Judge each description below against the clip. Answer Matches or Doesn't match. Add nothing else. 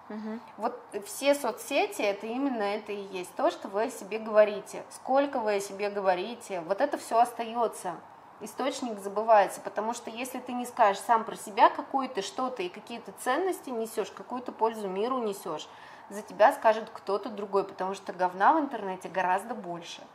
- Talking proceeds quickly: Matches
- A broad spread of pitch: Doesn't match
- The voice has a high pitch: Matches